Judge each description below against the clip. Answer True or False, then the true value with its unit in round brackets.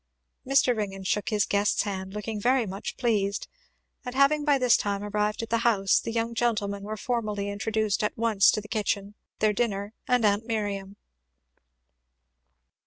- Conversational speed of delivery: True (165 wpm)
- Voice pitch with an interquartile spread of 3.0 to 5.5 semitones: False (2.4 semitones)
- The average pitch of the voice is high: True (210 Hz)